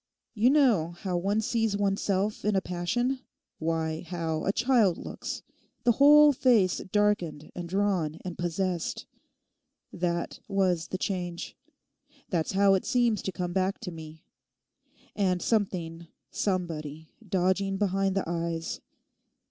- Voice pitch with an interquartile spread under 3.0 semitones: No, average, 3.4 semitones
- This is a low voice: No, high, 190 Hz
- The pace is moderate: No, slow, 125 wpm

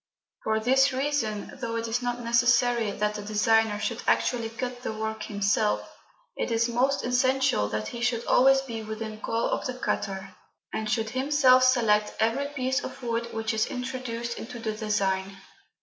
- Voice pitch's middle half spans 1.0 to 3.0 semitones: Yes, narrow, 2.6 semitones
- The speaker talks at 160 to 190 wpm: Yes, average, 170 wpm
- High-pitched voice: Yes, high, 230 Hz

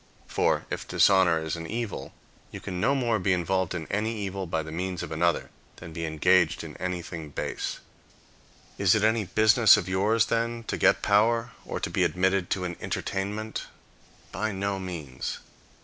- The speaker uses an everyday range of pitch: Yes, average, 3.9 semitones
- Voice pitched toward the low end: Yes, very low, 95 Hz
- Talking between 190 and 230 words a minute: No, average, 175 wpm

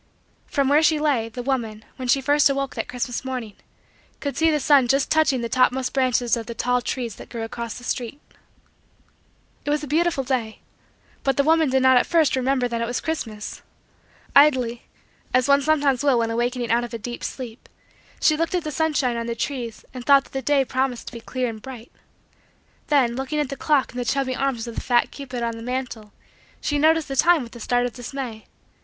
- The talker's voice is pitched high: Yes, very high, 255 Hz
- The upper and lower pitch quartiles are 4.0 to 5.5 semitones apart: No, average, 2.9 semitones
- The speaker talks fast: Yes, fast, 215 wpm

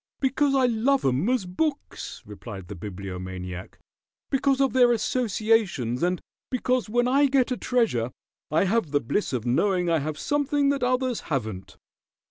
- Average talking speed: Yes, average, 155 wpm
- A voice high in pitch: Yes, high, 215 Hz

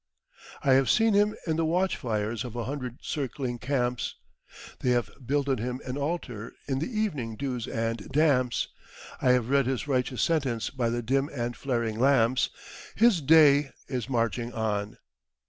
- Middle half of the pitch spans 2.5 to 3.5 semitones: Yes, average, 3.2 semitones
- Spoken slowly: No, average, 165 wpm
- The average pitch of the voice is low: Yes, low, 130 Hz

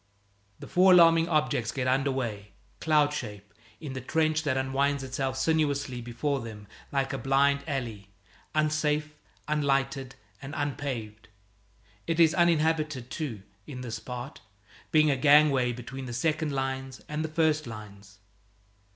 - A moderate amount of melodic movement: Yes, average, 3.5 semitones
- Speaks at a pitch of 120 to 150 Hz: Yes, medium, 140 Hz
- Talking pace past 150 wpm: No, average, 140 wpm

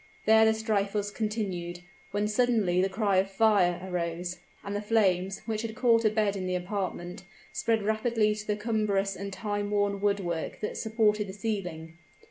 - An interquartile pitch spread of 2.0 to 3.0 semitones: Yes, narrow, 2.5 semitones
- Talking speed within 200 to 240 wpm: No, average, 175 wpm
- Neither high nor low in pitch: No, high, 205 Hz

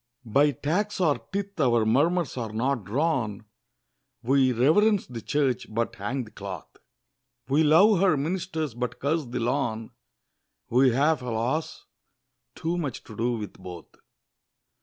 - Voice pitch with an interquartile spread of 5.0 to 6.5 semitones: Yes, wide, 5.6 semitones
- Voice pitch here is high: No, low, 135 Hz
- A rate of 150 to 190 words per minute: No, average, 140 wpm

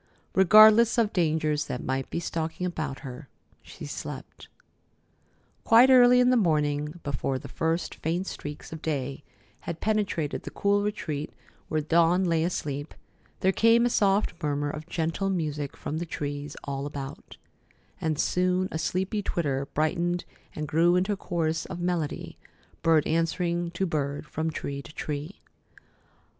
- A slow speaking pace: No, average, 150 wpm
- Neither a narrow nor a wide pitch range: Yes, average, 3.8 semitones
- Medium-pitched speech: Yes, medium, 165 Hz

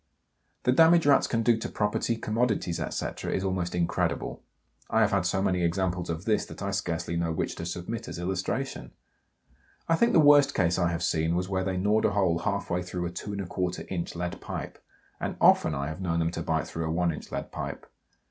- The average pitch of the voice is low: Yes, very low, 90 Hz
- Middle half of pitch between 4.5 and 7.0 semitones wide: No, average, 3.7 semitones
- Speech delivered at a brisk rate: Yes, fast, 215 wpm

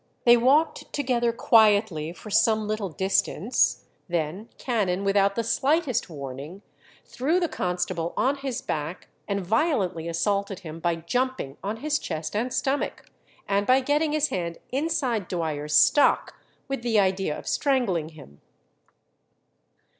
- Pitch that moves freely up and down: Yes, wide, 6.9 semitones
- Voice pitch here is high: Yes, high, 205 Hz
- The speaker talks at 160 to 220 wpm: No, slow, 135 wpm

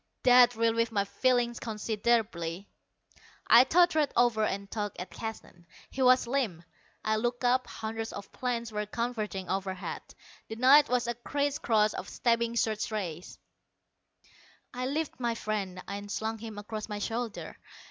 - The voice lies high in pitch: Yes, high, 225 Hz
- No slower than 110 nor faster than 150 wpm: Yes, average, 145 wpm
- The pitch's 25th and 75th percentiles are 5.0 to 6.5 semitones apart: No, average, 2.9 semitones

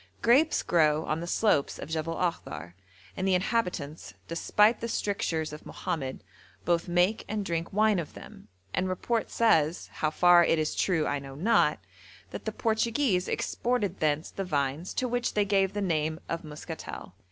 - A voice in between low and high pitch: Yes, medium, 175 Hz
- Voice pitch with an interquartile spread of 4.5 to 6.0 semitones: Yes, average, 5.0 semitones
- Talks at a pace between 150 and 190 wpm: Yes, average, 170 wpm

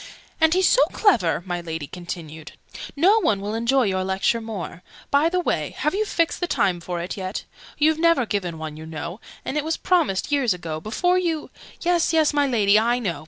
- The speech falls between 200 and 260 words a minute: Yes, fast, 205 wpm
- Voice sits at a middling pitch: No, high, 225 Hz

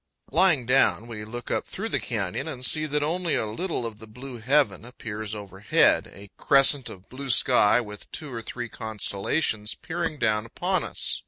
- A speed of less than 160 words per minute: No, average, 180 wpm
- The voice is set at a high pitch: No, low, 120 Hz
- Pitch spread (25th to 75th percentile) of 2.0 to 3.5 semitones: No, average, 5.0 semitones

